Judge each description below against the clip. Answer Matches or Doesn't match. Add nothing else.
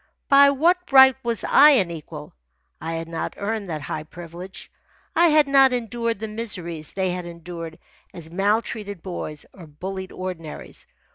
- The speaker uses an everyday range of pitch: Doesn't match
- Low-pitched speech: Doesn't match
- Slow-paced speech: Doesn't match